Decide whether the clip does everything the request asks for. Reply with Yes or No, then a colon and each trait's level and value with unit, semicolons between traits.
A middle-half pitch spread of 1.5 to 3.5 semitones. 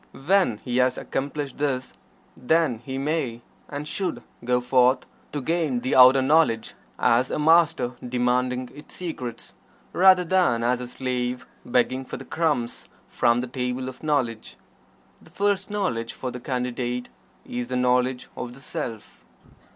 Yes: average, 3.2 semitones